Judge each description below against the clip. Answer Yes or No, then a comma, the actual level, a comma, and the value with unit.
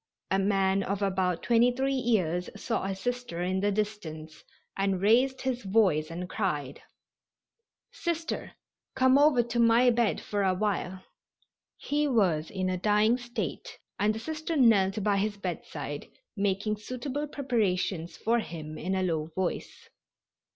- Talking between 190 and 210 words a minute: No, average, 140 wpm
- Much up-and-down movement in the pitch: No, average, 4.5 semitones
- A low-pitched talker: No, high, 205 Hz